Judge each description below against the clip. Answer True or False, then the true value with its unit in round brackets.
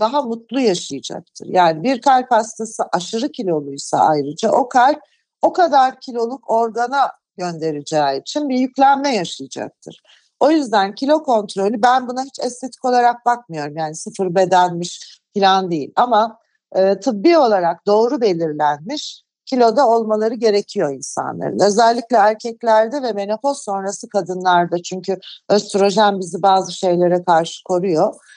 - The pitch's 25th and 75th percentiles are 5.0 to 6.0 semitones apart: True (5.6 semitones)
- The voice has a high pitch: True (215 Hz)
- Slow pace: False (125 wpm)